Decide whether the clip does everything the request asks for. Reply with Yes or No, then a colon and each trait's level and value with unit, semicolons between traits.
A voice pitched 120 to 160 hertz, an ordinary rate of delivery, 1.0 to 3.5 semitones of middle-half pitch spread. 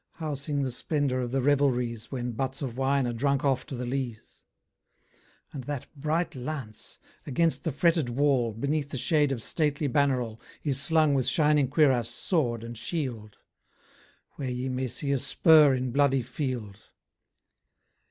Yes: low, 135 Hz; average, 160 wpm; average, 2.8 semitones